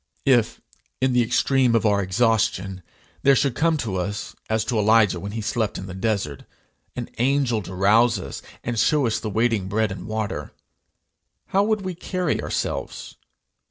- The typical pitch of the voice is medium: No, low, 110 Hz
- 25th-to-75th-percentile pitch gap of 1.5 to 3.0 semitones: No, average, 3.8 semitones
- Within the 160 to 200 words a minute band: Yes, average, 170 wpm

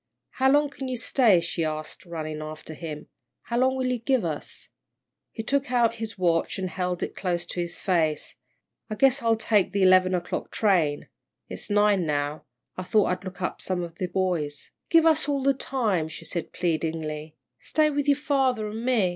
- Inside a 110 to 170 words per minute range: No, average, 195 wpm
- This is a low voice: No, high, 190 Hz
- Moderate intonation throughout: No, wide, 7.0 semitones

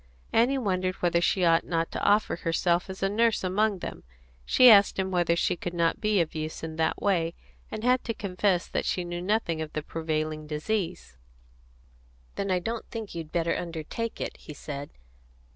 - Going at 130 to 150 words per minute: No, average, 190 wpm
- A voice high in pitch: No, medium, 175 Hz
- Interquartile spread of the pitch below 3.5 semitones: No, average, 3.8 semitones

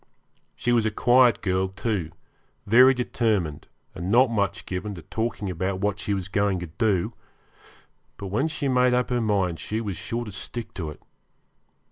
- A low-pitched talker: Yes, low, 105 Hz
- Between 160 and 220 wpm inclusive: Yes, average, 175 wpm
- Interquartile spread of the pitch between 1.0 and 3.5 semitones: No, average, 4.1 semitones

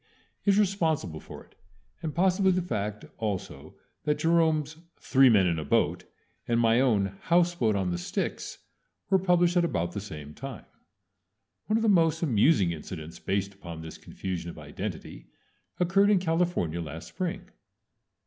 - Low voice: Yes, low, 130 Hz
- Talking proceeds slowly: No, average, 160 wpm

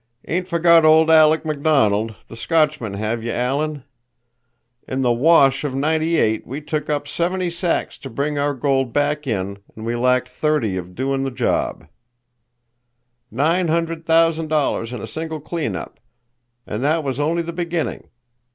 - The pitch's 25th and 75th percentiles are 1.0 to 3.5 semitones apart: No, average, 4.4 semitones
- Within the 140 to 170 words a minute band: Yes, average, 160 wpm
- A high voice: No, medium, 145 Hz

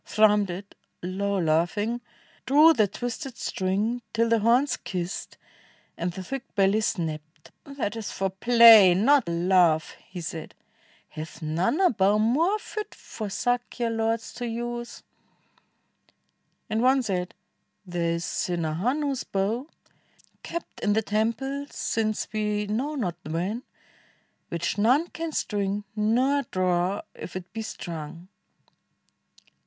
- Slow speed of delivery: Yes, slow, 130 wpm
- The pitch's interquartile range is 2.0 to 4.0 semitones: No, average, 4.9 semitones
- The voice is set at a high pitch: Yes, high, 210 Hz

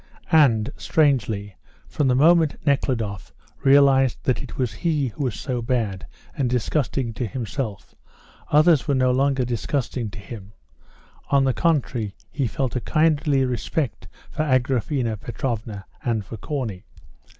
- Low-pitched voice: Yes, low, 130 Hz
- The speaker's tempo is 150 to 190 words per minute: No, average, 140 wpm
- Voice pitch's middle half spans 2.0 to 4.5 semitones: Yes, average, 3.9 semitones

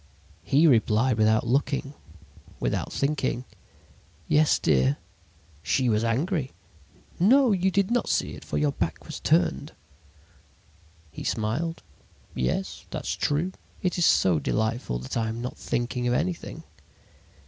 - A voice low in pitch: Yes, low, 125 Hz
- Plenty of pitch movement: Yes, wide, 7.0 semitones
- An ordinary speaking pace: No, slow, 130 wpm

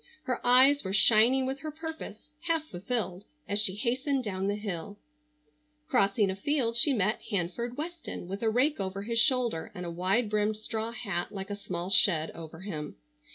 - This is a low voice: No, high, 215 Hz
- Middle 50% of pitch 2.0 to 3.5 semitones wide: No, average, 4.9 semitones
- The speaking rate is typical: Yes, average, 180 wpm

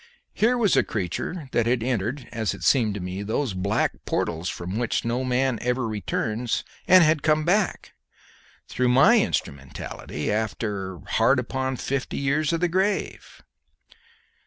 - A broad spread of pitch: Yes, wide, 5.9 semitones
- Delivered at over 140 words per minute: Yes, average, 150 wpm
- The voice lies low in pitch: Yes, low, 125 Hz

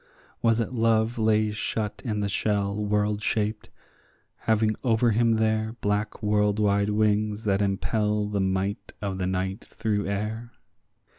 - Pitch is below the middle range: Yes, low, 105 Hz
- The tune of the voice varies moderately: No, narrow, 1.3 semitones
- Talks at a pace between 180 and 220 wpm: No, average, 145 wpm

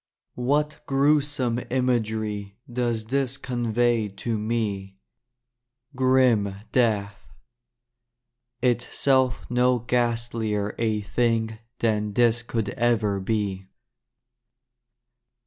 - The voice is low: Yes, low, 115 Hz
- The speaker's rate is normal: No, slow, 80 wpm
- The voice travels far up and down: No, narrow, 2.6 semitones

